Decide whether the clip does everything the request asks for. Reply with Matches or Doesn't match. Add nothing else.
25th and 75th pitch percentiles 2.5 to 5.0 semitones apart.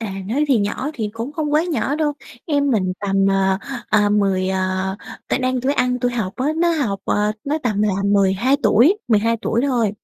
Doesn't match